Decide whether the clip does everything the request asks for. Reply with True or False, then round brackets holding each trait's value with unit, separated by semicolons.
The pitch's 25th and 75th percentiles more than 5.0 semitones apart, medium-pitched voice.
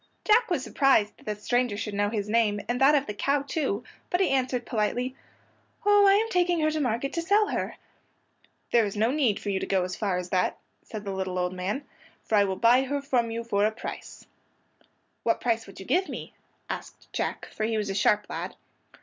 False (5.4 semitones; 230 Hz)